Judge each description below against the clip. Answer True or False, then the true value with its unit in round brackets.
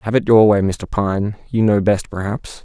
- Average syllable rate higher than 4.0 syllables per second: True (4.5 syllables/s)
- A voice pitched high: False (105 Hz)